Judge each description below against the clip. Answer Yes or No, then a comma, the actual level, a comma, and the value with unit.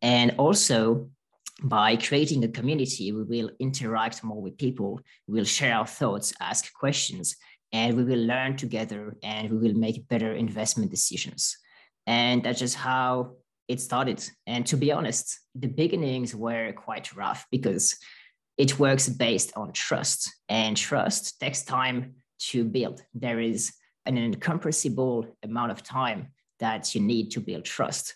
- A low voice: Yes, low, 120 Hz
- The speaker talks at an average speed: Yes, average, 150 wpm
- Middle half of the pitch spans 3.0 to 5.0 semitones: No, narrow, 2.4 semitones